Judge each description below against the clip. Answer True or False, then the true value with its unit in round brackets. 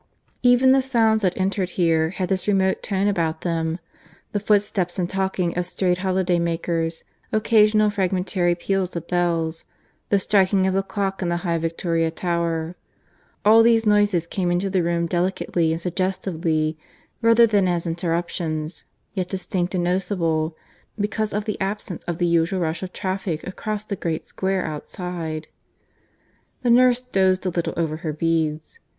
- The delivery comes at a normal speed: True (155 wpm)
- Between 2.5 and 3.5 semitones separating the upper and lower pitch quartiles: True (2.9 semitones)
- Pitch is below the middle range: False (180 Hz)